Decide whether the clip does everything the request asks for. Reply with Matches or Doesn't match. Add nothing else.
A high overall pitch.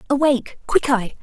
Matches